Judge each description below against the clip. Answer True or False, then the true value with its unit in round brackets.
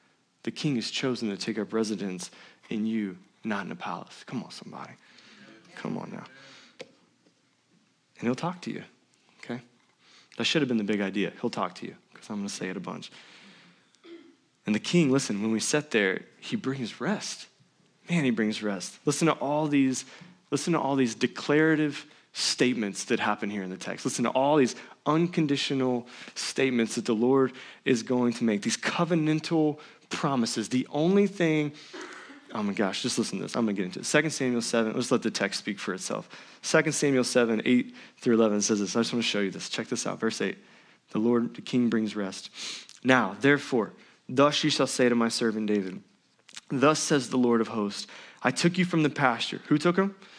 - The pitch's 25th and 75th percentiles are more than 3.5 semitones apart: True (5.2 semitones)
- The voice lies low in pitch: True (125 Hz)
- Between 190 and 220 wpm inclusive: True (200 wpm)